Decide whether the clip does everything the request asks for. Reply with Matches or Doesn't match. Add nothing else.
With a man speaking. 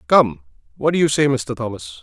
Matches